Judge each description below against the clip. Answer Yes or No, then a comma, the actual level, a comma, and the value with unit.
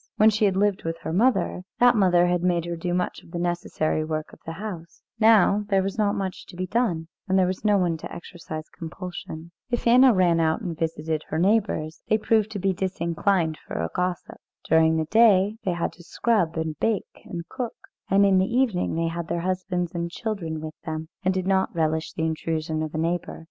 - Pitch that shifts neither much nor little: Yes, average, 3.5 semitones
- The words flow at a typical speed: No, fast, 215 wpm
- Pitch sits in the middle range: Yes, medium, 180 Hz